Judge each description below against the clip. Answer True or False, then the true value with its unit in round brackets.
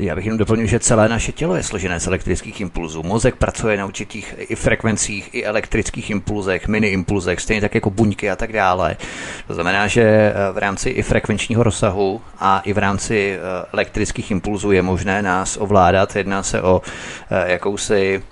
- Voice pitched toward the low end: True (105 Hz)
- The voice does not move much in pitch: True (2.3 semitones)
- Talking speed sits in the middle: False (175 wpm)